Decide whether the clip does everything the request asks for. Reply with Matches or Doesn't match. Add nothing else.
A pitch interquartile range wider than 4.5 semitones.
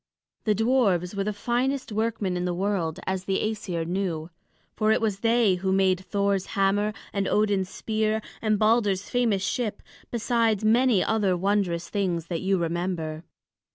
Doesn't match